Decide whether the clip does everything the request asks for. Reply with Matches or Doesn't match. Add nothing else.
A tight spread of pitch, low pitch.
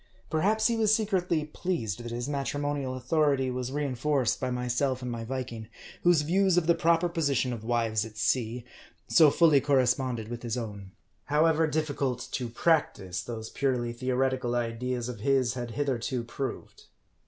Doesn't match